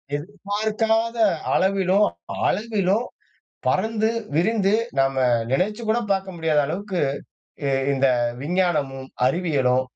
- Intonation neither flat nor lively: No, wide, 6.0 semitones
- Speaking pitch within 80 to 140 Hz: No, high, 190 Hz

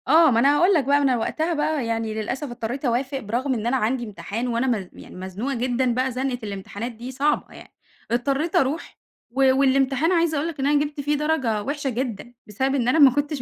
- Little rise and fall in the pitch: No, average, 3.6 semitones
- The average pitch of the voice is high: Yes, very high, 265 Hz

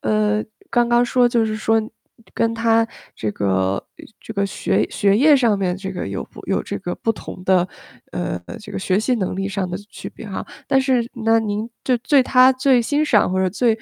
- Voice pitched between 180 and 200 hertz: No, high, 220 Hz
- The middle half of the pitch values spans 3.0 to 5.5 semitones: Yes, average, 4.0 semitones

